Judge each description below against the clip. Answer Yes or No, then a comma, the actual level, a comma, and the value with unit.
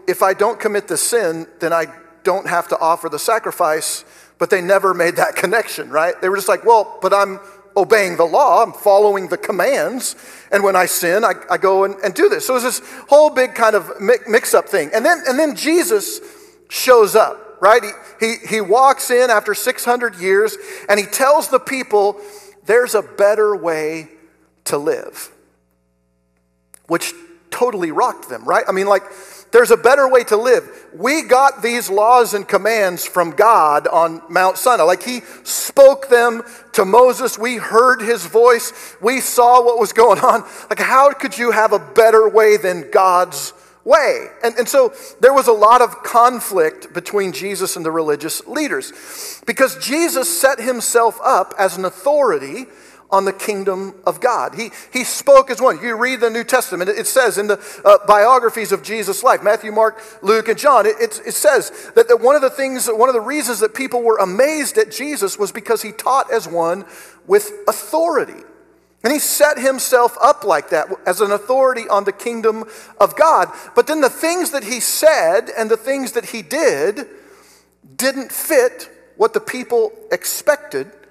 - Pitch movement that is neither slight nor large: No, wide, 7.2 semitones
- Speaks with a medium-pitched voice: No, high, 240 Hz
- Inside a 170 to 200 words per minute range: Yes, average, 185 wpm